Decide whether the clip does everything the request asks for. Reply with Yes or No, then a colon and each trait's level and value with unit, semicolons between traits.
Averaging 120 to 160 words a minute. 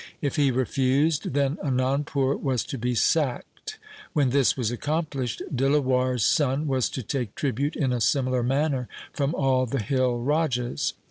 Yes: average, 155 wpm